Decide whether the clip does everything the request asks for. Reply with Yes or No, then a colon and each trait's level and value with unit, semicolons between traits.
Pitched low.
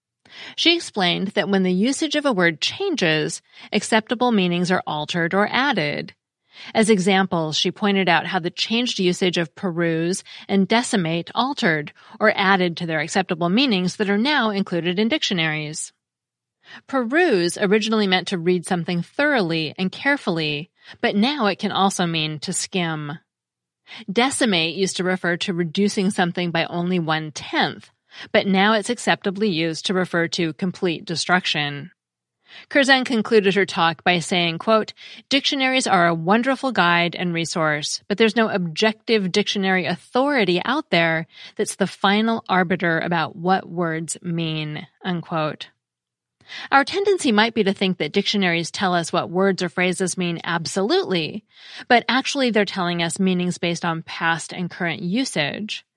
No: medium, 185 Hz